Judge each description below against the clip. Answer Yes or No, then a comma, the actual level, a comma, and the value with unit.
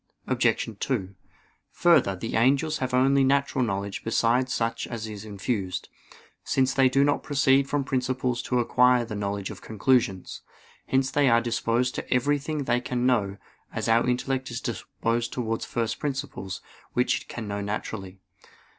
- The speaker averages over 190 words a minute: No, average, 155 wpm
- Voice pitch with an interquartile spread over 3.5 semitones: No, average, 3.1 semitones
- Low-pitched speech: Yes, low, 125 Hz